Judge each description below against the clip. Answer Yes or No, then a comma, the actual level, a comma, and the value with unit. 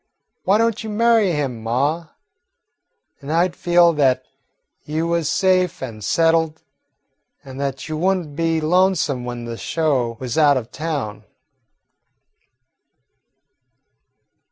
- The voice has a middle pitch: Yes, medium, 155 Hz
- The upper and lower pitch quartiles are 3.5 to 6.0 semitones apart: Yes, average, 4.8 semitones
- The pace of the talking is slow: Yes, slow, 125 wpm